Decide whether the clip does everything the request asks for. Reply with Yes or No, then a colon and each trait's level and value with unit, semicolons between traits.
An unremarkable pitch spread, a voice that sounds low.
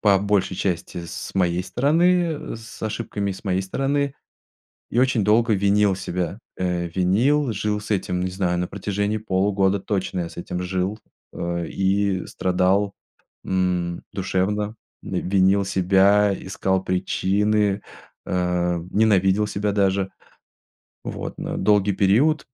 No: narrow, 2.2 semitones; very low, 95 Hz